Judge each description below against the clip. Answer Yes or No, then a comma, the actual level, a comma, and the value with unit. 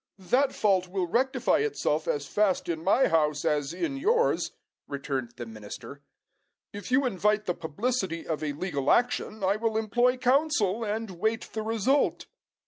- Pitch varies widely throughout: Yes, wide, 7.2 semitones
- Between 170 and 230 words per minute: No, average, 155 wpm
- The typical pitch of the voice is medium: No, high, 205 Hz